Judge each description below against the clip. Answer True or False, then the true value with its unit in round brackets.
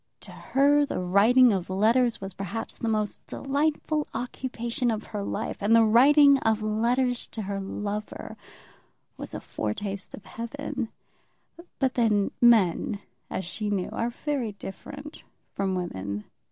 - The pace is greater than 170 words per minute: False (140 wpm)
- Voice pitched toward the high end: True (225 Hz)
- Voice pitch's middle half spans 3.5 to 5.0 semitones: True (4.2 semitones)